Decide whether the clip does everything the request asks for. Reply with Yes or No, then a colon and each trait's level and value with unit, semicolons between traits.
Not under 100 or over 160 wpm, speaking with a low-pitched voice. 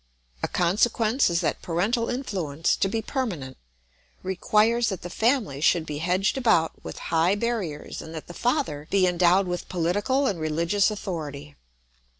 No: average, 155 wpm; medium, 185 Hz